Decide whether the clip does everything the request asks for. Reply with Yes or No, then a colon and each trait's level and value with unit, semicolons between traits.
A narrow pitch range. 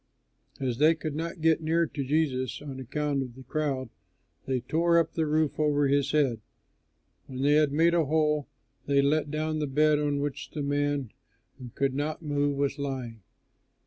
Yes: narrow, 2.2 semitones